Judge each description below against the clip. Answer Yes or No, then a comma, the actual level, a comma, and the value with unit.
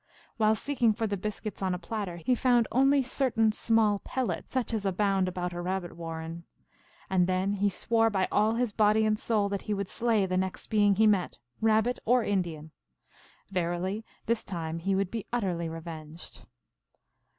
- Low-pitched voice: No, high, 200 Hz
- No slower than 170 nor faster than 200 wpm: Yes, average, 175 wpm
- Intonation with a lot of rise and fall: No, average, 3.7 semitones